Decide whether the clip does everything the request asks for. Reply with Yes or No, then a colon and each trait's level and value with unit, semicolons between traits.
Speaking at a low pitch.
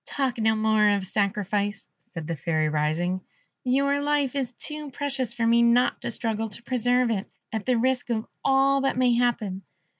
No: high, 235 Hz